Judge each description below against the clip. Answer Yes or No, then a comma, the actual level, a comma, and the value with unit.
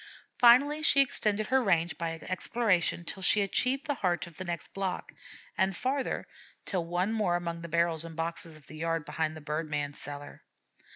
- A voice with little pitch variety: No, average, 4.5 semitones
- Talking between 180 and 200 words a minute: Yes, average, 185 wpm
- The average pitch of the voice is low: No, medium, 175 Hz